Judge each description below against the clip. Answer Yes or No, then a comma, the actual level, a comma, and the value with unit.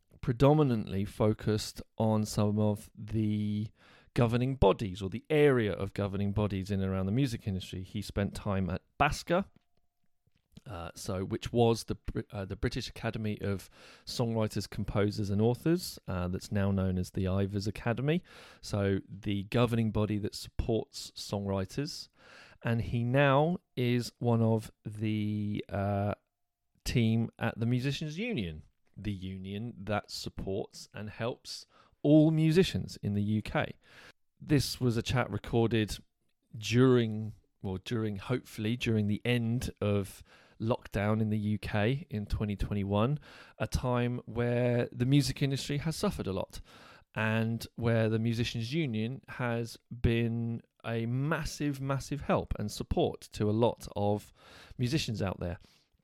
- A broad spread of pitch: No, average, 3.3 semitones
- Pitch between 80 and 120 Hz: Yes, low, 110 Hz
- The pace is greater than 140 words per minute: No, slow, 135 wpm